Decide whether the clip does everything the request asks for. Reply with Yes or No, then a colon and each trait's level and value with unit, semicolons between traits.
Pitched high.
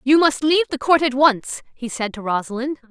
Yes: very high, 265 Hz